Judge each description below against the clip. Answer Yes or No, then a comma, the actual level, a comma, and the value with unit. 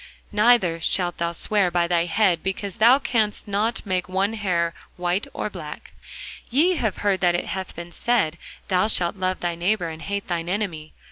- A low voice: No, medium, 185 Hz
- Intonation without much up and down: No, average, 3.4 semitones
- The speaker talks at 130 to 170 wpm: No, average, 185 wpm